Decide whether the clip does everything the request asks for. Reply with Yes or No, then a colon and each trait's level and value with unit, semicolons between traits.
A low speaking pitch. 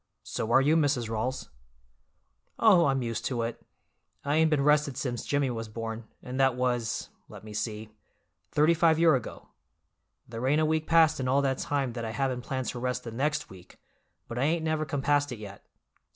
Yes: low, 130 Hz